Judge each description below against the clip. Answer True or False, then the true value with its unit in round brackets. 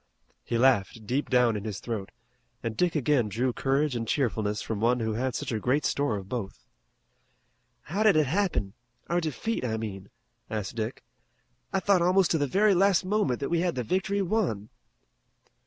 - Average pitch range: False (7.7 semitones)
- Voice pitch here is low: True (130 Hz)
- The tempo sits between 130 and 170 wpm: False (185 wpm)